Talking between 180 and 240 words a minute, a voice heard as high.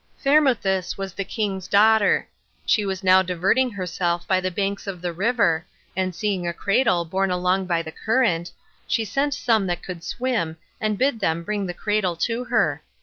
Yes: average, 185 wpm; high, 195 Hz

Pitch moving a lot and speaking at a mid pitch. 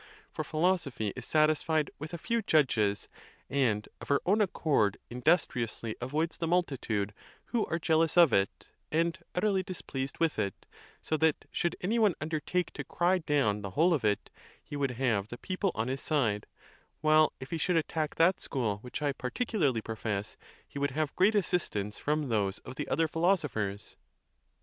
Yes: wide, 6.4 semitones; medium, 150 Hz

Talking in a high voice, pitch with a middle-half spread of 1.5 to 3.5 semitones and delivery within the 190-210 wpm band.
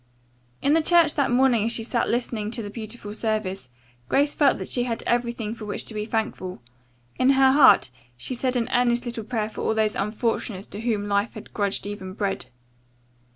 Yes: high, 225 Hz; average, 2.8 semitones; average, 195 wpm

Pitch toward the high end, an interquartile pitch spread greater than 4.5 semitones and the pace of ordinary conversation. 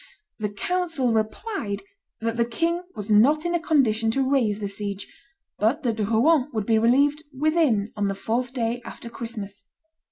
Yes: high, 230 Hz; average, 5.1 semitones; average, 165 wpm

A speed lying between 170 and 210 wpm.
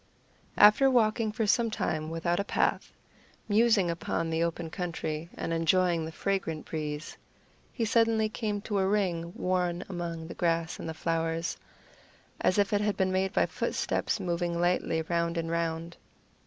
No: average, 160 wpm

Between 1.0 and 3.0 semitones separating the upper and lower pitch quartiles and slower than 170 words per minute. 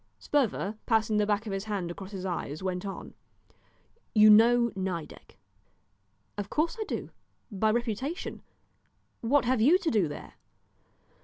No: average, 3.8 semitones; average, 145 wpm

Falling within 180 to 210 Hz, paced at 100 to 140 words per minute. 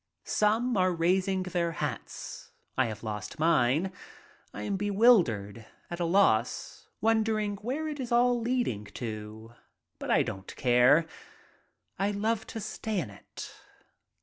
Yes: medium, 185 Hz; slow, 135 wpm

